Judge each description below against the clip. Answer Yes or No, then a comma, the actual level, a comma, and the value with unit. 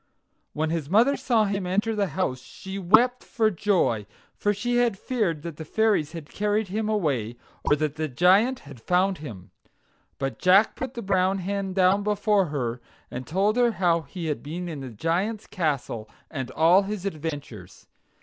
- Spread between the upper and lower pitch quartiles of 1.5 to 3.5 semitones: No, wide, 5.6 semitones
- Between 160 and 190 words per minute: Yes, average, 180 wpm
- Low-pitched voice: No, medium, 185 Hz